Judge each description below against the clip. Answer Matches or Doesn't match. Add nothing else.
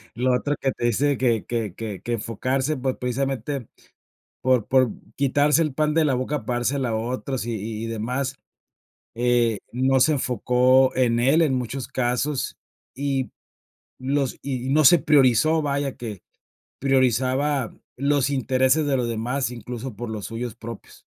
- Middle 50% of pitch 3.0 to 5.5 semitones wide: Doesn't match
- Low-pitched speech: Matches